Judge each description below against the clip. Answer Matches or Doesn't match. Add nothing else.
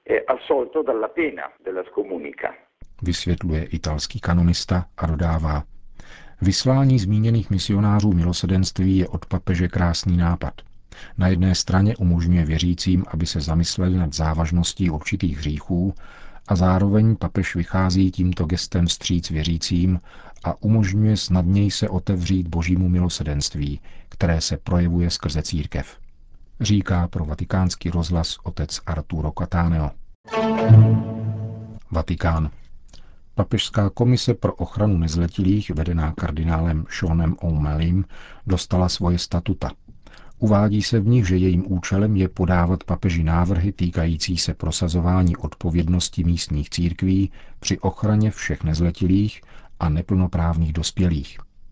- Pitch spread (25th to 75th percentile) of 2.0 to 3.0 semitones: Matches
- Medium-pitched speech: Doesn't match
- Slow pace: Matches